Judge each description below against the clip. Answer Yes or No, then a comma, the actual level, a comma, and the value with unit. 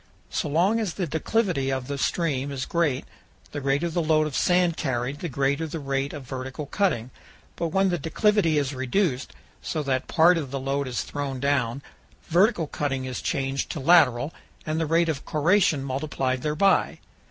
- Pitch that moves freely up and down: No, average, 3.8 semitones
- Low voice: No, medium, 145 Hz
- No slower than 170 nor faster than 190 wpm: Yes, average, 180 wpm